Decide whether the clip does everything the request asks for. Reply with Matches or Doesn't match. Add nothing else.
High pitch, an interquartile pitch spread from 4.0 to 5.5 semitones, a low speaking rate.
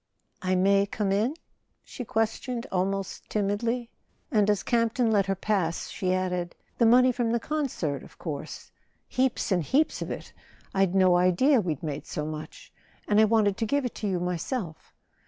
Doesn't match